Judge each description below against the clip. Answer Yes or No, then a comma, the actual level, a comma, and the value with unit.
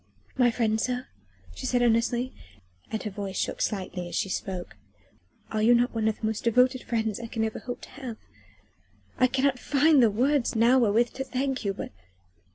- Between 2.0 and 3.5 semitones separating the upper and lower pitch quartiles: Yes, average, 2.7 semitones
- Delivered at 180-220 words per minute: Yes, average, 190 wpm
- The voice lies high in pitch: Yes, high, 235 Hz